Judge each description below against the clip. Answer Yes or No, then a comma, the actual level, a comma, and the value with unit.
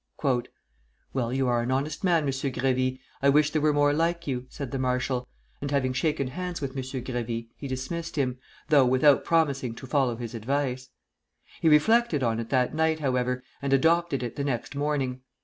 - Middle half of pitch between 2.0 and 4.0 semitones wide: Yes, average, 2.8 semitones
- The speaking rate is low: No, average, 185 wpm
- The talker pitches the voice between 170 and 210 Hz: No, low, 135 Hz